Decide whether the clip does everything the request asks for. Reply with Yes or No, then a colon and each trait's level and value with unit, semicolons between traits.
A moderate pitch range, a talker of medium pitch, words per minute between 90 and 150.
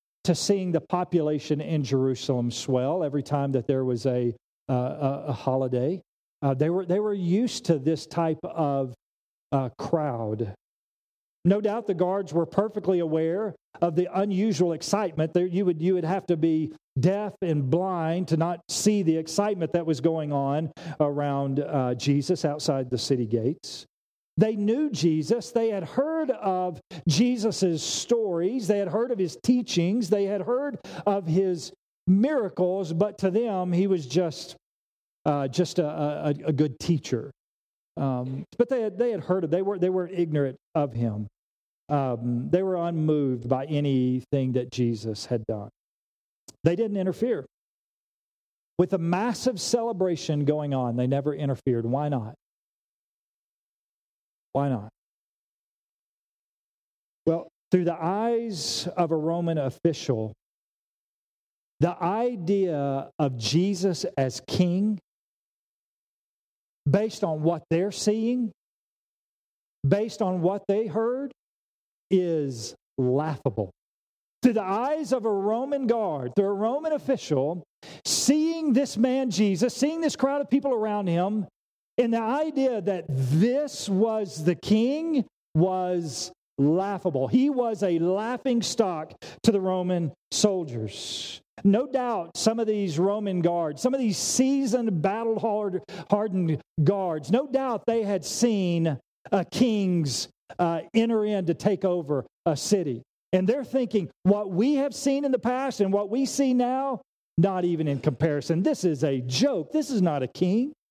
No: wide, 6.2 semitones; medium, 180 Hz; average, 145 wpm